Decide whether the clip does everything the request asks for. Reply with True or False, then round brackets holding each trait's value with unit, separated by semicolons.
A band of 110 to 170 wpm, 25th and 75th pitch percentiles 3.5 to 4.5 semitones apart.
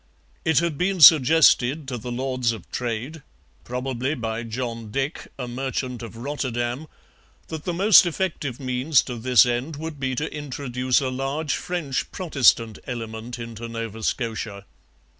True (145 wpm; 3.8 semitones)